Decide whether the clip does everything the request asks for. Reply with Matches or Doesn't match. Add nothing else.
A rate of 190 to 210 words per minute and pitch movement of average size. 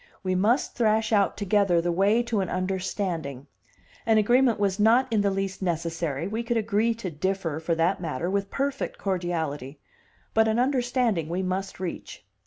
Doesn't match